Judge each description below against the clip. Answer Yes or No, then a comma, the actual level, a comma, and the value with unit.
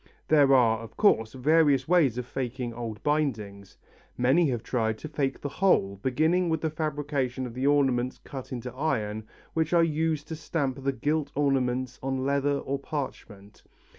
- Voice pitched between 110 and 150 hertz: Yes, low, 135 Hz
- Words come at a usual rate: Yes, average, 165 wpm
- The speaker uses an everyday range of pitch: Yes, average, 3.6 semitones